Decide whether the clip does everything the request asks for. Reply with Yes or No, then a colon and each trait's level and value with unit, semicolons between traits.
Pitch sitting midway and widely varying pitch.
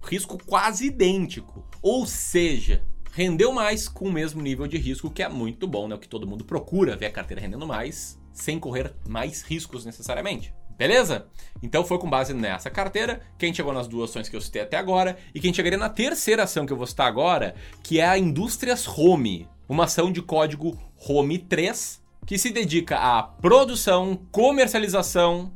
Yes: medium, 170 Hz; wide, 7.0 semitones